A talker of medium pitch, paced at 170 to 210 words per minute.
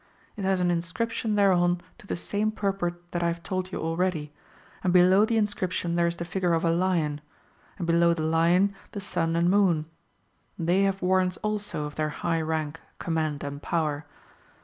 Yes: medium, 175 Hz; average, 185 wpm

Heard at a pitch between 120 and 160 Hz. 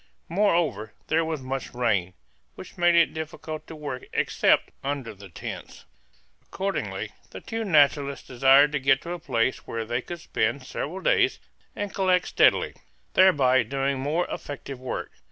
Yes: medium, 140 Hz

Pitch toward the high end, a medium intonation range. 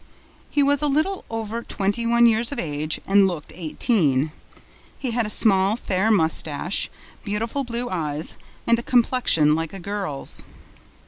No: high, 210 Hz; wide, 6.5 semitones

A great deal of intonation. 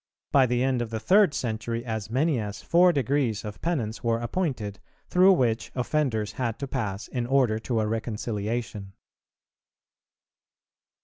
No: average, 3.8 semitones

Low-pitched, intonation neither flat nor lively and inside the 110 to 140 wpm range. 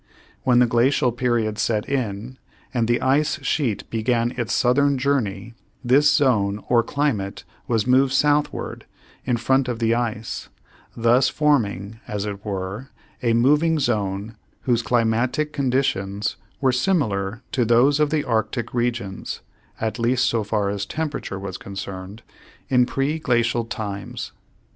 Yes: low, 120 Hz; average, 3.8 semitones; slow, 135 wpm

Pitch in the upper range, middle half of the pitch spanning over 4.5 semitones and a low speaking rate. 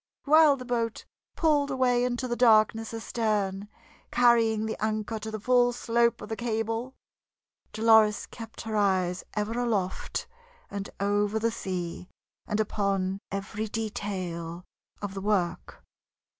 No: high, 220 Hz; average, 2.9 semitones; slow, 130 wpm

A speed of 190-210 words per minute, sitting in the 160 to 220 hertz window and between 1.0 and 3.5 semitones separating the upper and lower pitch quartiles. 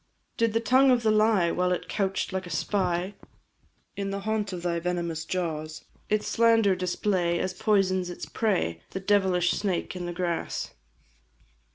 No: average, 165 wpm; medium, 185 Hz; average, 3.0 semitones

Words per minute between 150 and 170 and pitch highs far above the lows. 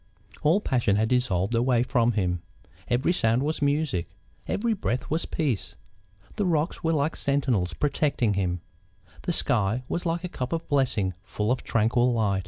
Yes: average, 165 wpm; wide, 6.0 semitones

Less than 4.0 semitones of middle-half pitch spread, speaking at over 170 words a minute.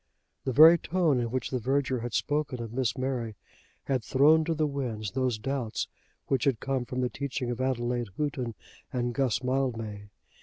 Yes: narrow, 2.4 semitones; average, 180 wpm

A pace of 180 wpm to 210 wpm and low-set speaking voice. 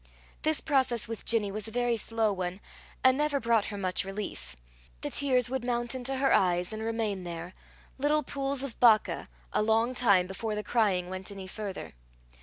No: average, 185 wpm; high, 225 Hz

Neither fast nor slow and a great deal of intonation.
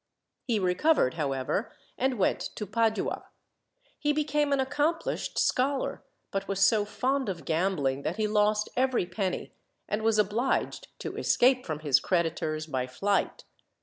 Yes: average, 145 wpm; wide, 7.1 semitones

